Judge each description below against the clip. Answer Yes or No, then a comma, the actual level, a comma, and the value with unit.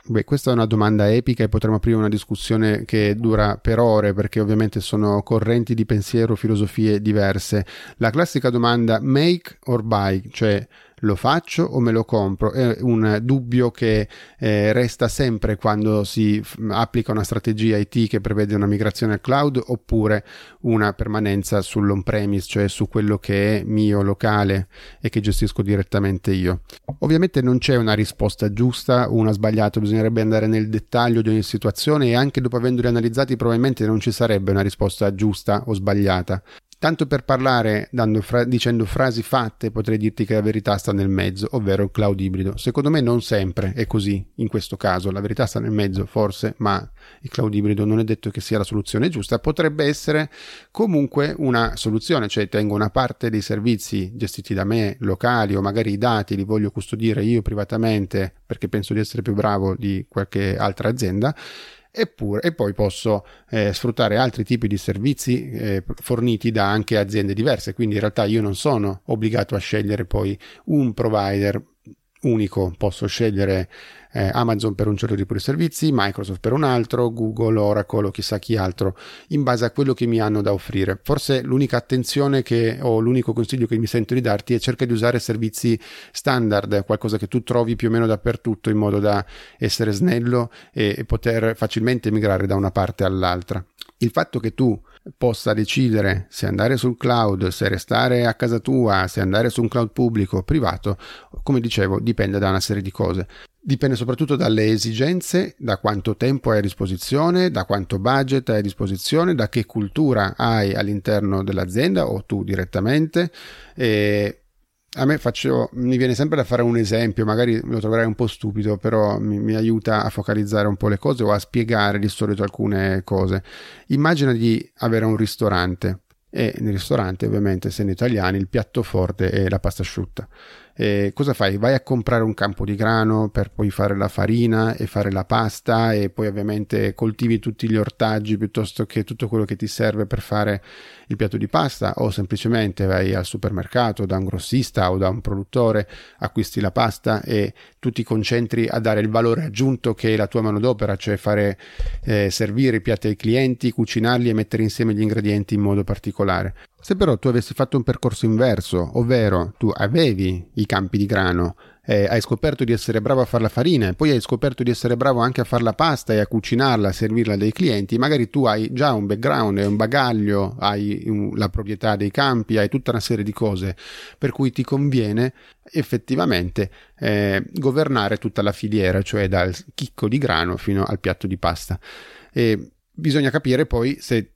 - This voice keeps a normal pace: No, fast, 185 wpm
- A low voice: Yes, low, 110 Hz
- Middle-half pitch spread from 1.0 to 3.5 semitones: Yes, average, 2.9 semitones